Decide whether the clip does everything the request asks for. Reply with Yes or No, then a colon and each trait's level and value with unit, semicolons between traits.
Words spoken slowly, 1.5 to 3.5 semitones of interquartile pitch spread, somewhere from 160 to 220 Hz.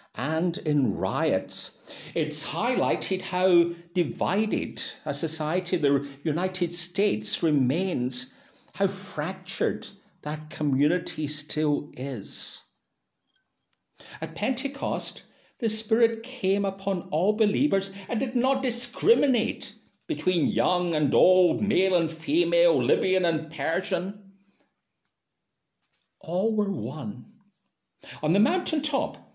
No: slow, 100 wpm; wide, 5.4 semitones; medium, 185 Hz